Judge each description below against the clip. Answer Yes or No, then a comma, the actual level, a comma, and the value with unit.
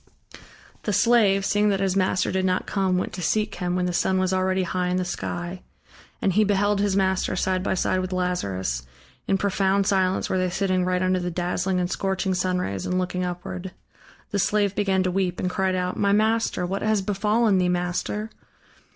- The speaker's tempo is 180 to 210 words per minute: Yes, average, 200 wpm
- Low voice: No, medium, 185 Hz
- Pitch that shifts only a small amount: Yes, narrow, 1.5 semitones